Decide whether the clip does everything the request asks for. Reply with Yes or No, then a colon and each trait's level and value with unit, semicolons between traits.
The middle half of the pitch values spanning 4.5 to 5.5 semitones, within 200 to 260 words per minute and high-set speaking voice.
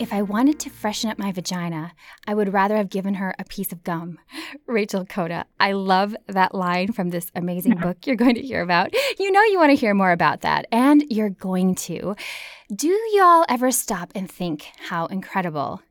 Yes: average, 5.0 semitones; fast, 205 wpm; high, 200 Hz